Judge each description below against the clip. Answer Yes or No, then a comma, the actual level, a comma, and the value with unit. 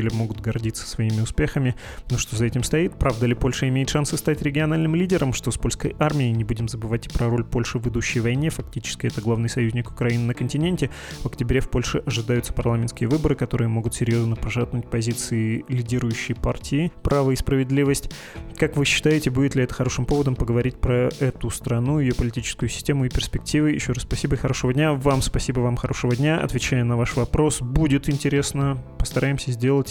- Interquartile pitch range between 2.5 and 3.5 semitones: Yes, average, 3.0 semitones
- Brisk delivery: Yes, fast, 185 wpm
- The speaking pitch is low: Yes, low, 125 Hz